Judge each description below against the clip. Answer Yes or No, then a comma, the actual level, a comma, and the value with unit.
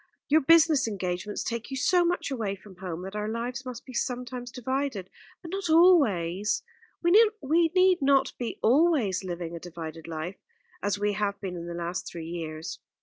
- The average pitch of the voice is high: Yes, high, 220 Hz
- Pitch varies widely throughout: Yes, wide, 7.8 semitones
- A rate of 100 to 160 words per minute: No, average, 175 wpm